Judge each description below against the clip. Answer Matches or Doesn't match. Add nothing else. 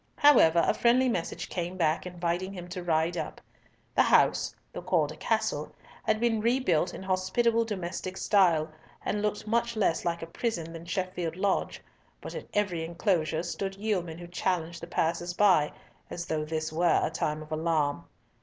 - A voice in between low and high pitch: Matches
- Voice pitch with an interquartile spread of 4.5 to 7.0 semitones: Doesn't match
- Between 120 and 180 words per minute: Matches